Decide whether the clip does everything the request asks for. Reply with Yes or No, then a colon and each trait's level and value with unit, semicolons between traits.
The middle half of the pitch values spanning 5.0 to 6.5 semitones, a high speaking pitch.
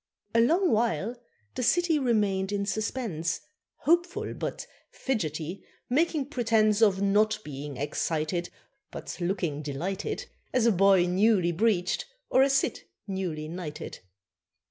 Yes: wide, 5.4 semitones; high, 200 Hz